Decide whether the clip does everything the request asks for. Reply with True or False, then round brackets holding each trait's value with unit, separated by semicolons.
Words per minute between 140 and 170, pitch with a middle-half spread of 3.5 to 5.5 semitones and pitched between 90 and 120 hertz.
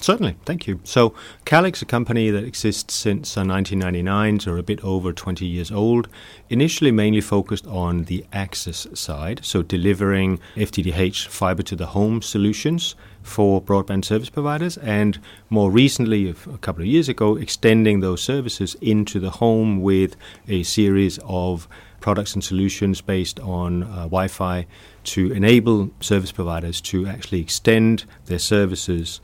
False (150 wpm; 2.8 semitones; 100 Hz)